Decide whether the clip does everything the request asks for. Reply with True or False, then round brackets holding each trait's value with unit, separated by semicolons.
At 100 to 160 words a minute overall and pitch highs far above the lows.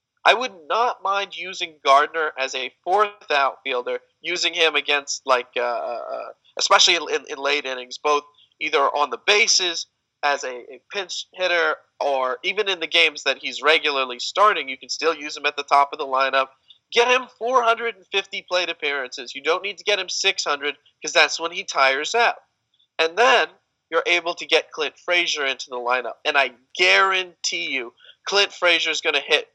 False (180 wpm; 6.1 semitones)